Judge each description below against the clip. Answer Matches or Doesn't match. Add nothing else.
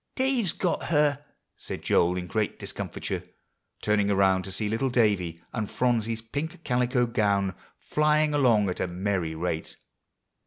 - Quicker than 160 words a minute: Doesn't match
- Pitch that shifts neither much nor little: Doesn't match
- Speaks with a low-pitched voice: Matches